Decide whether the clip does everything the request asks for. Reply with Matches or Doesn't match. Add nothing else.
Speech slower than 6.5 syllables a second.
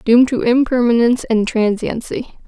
Matches